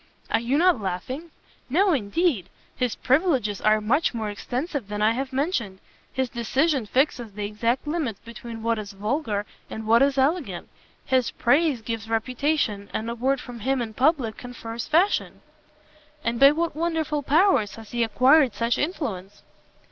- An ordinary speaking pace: Yes, average, 160 wpm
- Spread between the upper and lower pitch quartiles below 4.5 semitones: No, average, 4.9 semitones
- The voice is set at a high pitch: Yes, high, 245 Hz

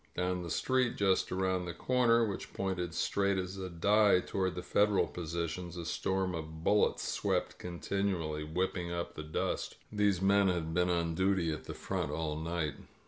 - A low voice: Yes, very low, 90 Hz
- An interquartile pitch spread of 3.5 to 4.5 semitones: No, average, 2.7 semitones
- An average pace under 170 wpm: No, average, 175 wpm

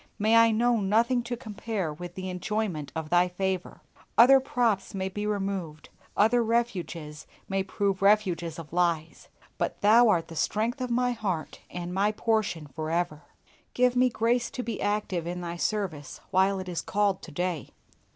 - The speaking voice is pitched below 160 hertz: No, high, 195 Hz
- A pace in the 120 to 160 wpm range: No, average, 170 wpm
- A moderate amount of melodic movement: Yes, average, 4.4 semitones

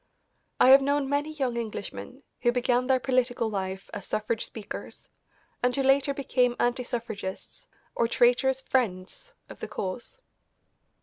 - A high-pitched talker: Yes, very high, 250 Hz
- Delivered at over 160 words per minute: No, average, 140 wpm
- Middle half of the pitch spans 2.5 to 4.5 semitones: Yes, average, 2.9 semitones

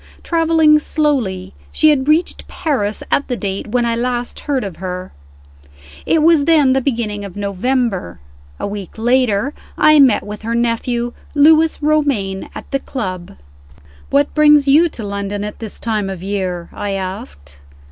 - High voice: Yes, high, 235 Hz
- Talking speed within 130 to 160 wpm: Yes, average, 155 wpm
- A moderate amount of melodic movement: No, wide, 6.4 semitones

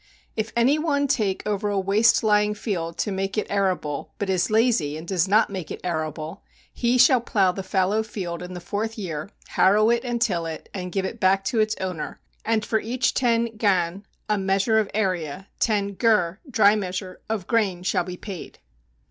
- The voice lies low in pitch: No, high, 200 Hz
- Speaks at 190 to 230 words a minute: Yes, average, 195 wpm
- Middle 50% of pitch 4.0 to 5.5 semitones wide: No, average, 3.3 semitones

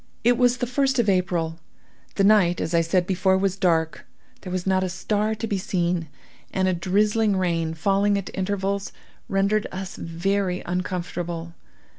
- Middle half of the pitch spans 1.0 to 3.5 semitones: Yes, narrow, 2.5 semitones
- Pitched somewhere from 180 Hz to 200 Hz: Yes, high, 190 Hz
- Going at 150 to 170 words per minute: Yes, average, 165 wpm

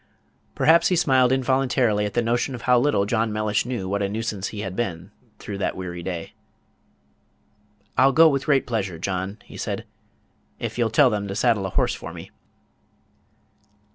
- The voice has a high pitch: No, low, 110 Hz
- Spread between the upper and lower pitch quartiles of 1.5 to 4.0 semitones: No, average, 4.4 semitones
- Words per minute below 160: No, average, 180 wpm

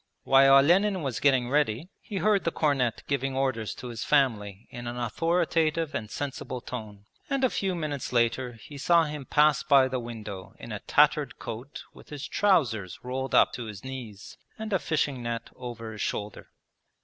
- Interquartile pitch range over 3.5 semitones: Yes, average, 4.7 semitones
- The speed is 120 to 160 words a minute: No, average, 180 wpm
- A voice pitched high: No, low, 130 Hz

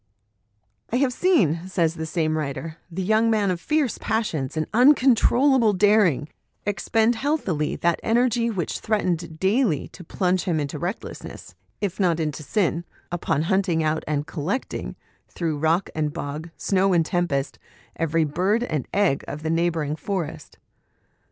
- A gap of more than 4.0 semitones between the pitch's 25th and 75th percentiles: Yes, average, 5.2 semitones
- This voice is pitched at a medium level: Yes, medium, 175 Hz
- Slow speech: No, average, 155 wpm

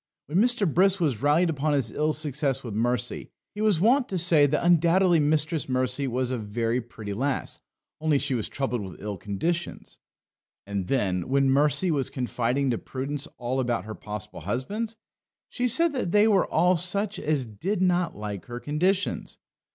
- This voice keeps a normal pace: Yes, average, 175 wpm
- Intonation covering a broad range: Yes, wide, 6.5 semitones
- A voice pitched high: No, medium, 145 Hz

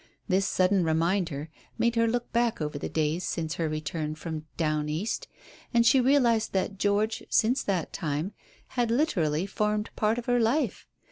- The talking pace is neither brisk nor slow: Yes, average, 165 wpm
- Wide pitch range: Yes, wide, 6.5 semitones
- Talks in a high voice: Yes, high, 195 Hz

